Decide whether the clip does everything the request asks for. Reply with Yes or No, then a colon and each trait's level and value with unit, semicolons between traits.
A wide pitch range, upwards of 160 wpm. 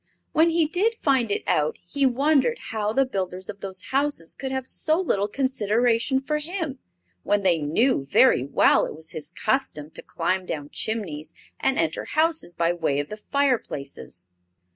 Yes: wide, 8.7 semitones; average, 170 wpm